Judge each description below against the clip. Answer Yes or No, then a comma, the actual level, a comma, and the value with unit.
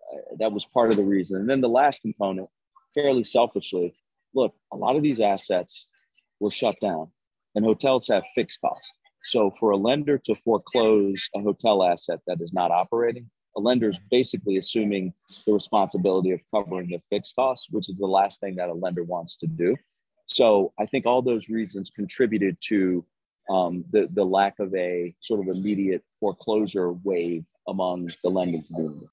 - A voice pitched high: No, low, 100 Hz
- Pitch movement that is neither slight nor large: Yes, average, 3.6 semitones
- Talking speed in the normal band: Yes, average, 175 wpm